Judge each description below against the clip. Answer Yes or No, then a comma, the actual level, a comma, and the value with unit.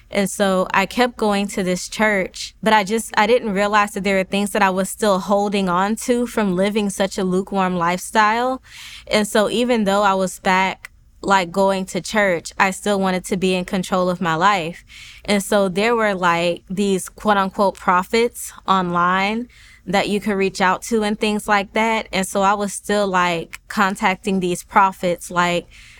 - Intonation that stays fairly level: Yes, narrow, 2.0 semitones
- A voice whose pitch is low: No, high, 200 Hz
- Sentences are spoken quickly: No, average, 185 wpm